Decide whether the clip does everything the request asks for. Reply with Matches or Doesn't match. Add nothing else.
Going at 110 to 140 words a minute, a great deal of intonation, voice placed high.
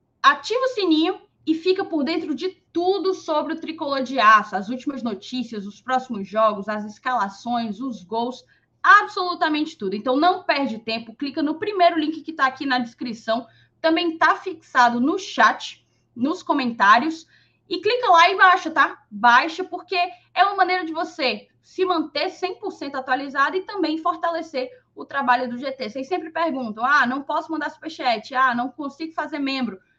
Doesn't match